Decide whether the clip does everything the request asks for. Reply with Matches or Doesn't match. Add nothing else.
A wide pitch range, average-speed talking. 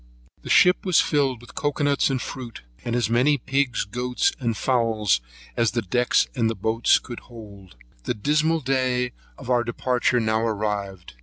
Doesn't match